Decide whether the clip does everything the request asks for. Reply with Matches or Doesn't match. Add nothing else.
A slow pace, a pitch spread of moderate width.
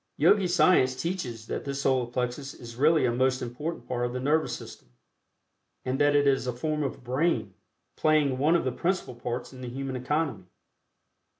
Doesn't match